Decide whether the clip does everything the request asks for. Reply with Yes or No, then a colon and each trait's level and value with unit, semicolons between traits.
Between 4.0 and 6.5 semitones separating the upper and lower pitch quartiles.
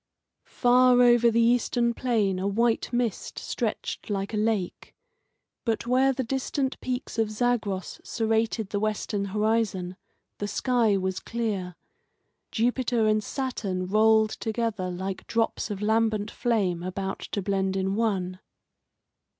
No: average, 3.3 semitones